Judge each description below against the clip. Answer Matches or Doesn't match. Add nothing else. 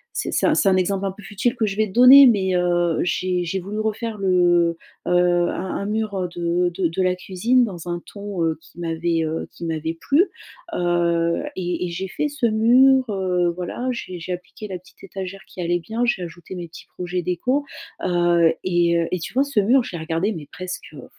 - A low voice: Doesn't match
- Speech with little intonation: Doesn't match